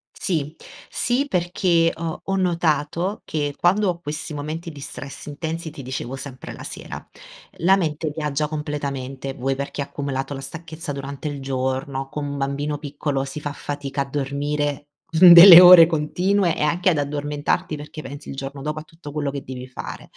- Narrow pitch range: No, average, 3.0 semitones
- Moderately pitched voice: Yes, medium, 150 Hz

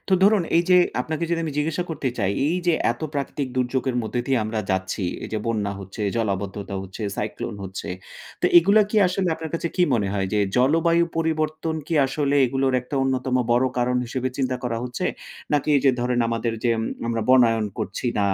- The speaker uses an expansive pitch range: Yes, wide, 5.9 semitones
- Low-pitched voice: Yes, low, 130 Hz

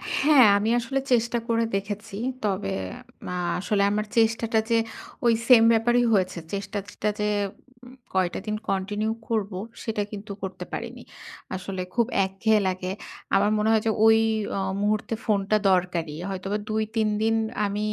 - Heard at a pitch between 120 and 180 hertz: No, high, 210 Hz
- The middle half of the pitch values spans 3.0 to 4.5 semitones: No, narrow, 2.5 semitones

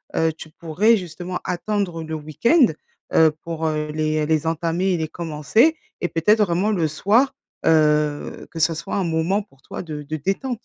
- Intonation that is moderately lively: Yes, average, 3.7 semitones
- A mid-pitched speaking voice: Yes, medium, 165 Hz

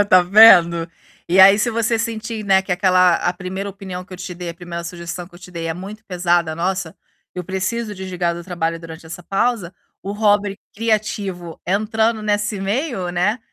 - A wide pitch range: No, average, 3.1 semitones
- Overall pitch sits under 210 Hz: Yes, high, 190 Hz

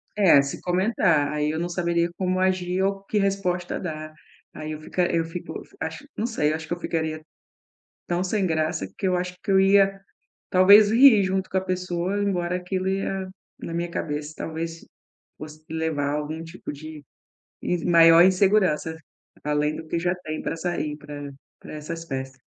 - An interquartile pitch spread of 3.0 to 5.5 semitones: Yes, average, 3.3 semitones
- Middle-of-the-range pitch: Yes, medium, 175 Hz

